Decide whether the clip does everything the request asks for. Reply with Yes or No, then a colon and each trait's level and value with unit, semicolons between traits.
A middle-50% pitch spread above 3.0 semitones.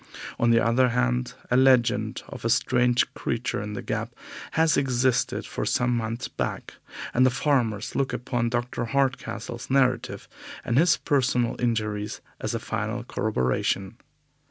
No: narrow, 2.4 semitones